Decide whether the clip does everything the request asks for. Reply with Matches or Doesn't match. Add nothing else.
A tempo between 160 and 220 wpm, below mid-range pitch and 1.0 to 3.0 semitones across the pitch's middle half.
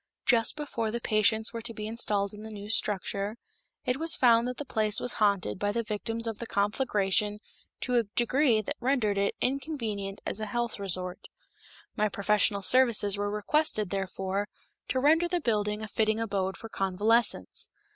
Doesn't match